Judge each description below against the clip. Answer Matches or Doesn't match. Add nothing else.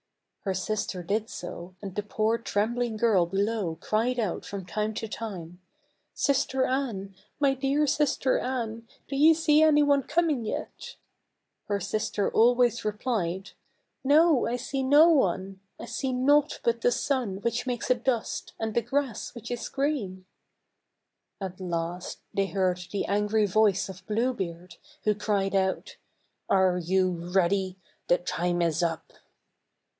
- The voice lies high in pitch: Matches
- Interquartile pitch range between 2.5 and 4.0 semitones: Doesn't match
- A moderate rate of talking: Matches